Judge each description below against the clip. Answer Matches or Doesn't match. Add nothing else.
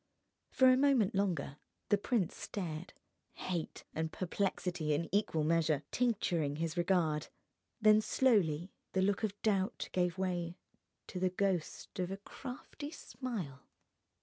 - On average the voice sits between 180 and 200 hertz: Matches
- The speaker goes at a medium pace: Doesn't match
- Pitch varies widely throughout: Doesn't match